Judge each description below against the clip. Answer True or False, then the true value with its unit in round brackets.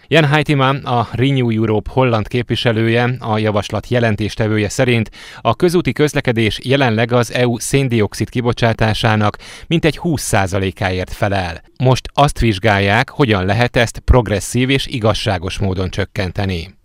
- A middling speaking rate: True (120 wpm)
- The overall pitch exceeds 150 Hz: False (115 Hz)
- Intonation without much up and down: False (3.7 semitones)